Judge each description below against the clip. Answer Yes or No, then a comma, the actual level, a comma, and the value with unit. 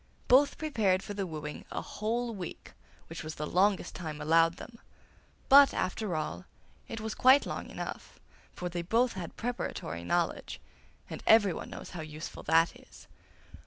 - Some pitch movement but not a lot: No, wide, 5.7 semitones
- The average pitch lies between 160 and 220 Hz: Yes, medium, 185 Hz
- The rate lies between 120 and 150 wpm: No, average, 160 wpm